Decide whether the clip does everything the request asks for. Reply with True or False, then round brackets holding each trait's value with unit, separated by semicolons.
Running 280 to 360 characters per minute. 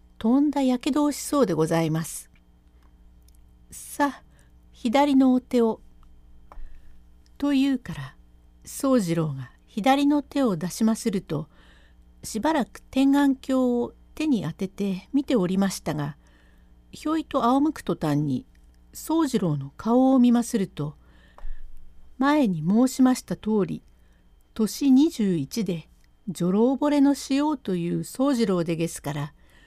False (235 characters per minute)